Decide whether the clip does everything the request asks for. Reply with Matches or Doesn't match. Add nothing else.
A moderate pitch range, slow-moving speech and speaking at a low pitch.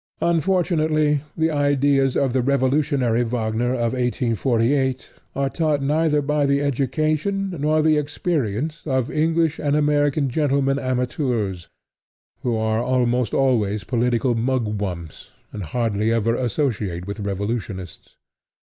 Matches